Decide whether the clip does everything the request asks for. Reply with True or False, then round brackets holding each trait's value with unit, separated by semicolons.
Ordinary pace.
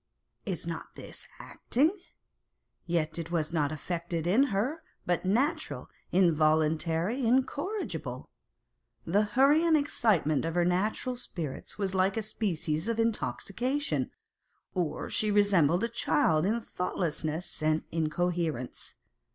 False (125 wpm)